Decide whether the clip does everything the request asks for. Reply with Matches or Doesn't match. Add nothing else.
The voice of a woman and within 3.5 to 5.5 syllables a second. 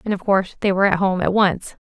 Doesn't match